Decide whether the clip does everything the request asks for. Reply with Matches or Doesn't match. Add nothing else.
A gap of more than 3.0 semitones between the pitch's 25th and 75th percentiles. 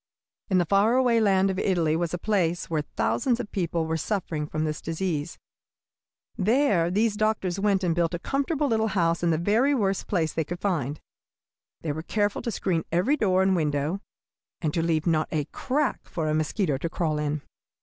Matches